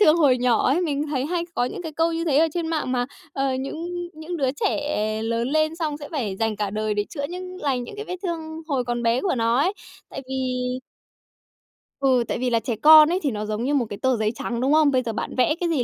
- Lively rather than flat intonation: No, average, 4.9 semitones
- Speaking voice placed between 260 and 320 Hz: Yes, very high, 275 Hz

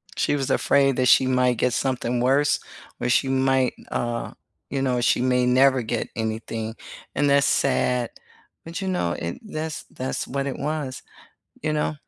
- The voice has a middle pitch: No, low, 130 Hz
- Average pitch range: No, narrow, 2.3 semitones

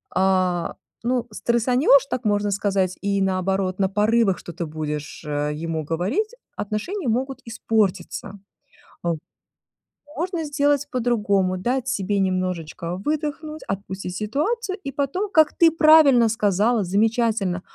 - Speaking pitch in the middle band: No, high, 210 Hz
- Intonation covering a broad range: Yes, wide, 6.3 semitones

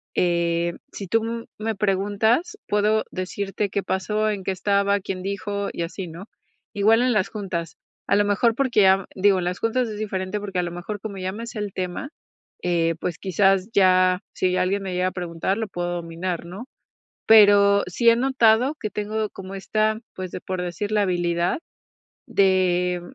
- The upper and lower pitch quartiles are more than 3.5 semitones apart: No, average, 2.7 semitones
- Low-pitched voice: No, high, 195 Hz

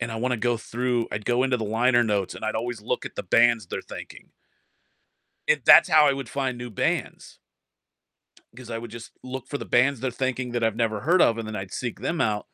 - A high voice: No, low, 120 Hz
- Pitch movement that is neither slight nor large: No, narrow, 2.3 semitones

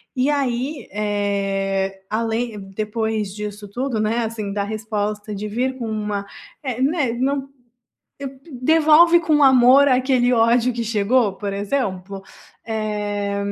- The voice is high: Yes, high, 220 Hz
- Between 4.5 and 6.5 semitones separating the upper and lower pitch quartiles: No, average, 3.8 semitones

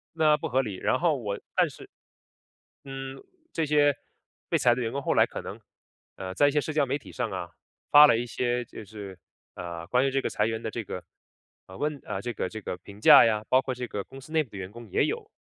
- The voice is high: No, low, 125 Hz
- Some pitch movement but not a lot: Yes, average, 4.9 semitones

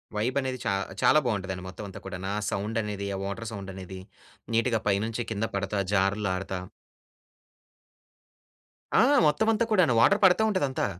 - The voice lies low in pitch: Yes, low, 105 Hz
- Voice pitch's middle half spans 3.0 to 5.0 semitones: Yes, average, 4.0 semitones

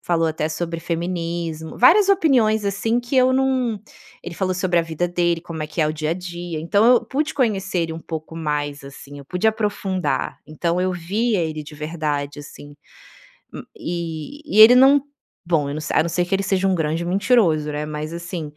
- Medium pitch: Yes, medium, 175 Hz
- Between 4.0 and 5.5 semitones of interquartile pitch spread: Yes, average, 4.5 semitones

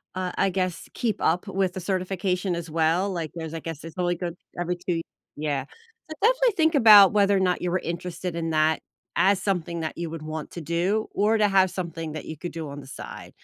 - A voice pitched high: No, medium, 175 Hz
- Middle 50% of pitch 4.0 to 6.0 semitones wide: No, average, 2.8 semitones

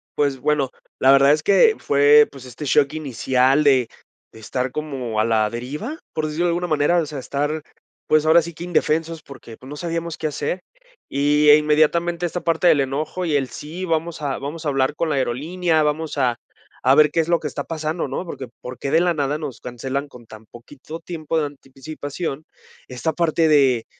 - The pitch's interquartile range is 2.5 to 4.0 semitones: Yes, average, 3.2 semitones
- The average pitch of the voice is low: No, medium, 150 Hz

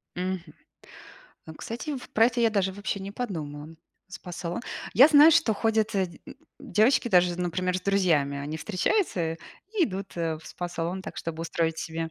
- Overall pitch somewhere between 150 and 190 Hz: Yes, medium, 185 Hz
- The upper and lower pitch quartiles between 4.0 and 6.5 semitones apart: Yes, average, 4.8 semitones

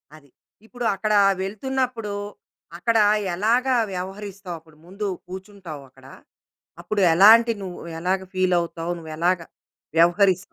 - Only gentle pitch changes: No, average, 3.6 semitones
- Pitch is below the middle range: No, high, 190 Hz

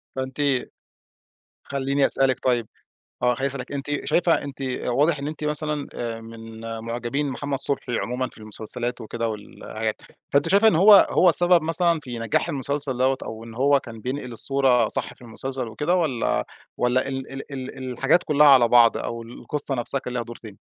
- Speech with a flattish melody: No, average, 3.3 semitones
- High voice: No, low, 130 Hz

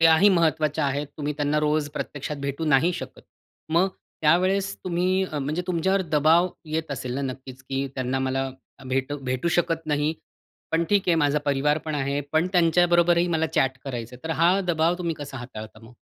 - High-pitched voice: No, medium, 150 Hz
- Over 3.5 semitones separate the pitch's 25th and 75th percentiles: Yes, average, 4.0 semitones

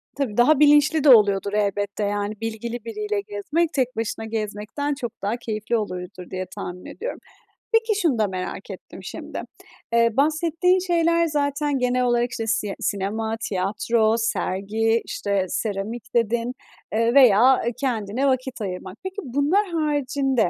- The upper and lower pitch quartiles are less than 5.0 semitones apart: No, wide, 5.4 semitones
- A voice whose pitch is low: No, high, 230 Hz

